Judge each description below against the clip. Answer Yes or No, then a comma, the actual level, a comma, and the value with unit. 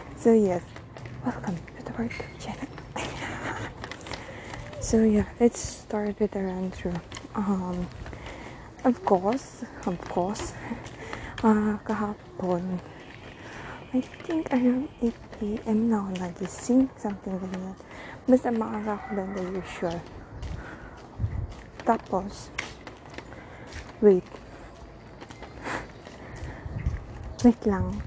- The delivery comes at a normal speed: No, slow, 95 wpm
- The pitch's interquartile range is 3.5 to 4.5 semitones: Yes, average, 3.8 semitones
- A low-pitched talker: No, high, 205 Hz